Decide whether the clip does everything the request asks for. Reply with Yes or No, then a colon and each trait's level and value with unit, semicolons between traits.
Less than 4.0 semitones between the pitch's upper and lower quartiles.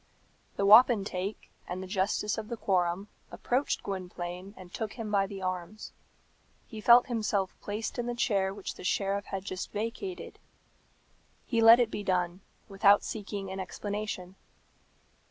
Yes: average, 2.7 semitones